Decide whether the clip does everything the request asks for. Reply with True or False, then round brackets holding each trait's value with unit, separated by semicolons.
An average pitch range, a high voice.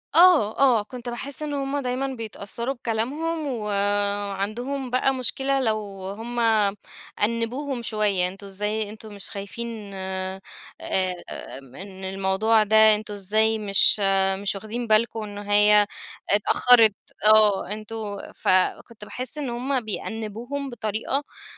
True (3.4 semitones; 220 Hz)